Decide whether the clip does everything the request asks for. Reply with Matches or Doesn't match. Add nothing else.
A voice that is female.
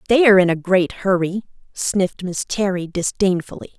Matches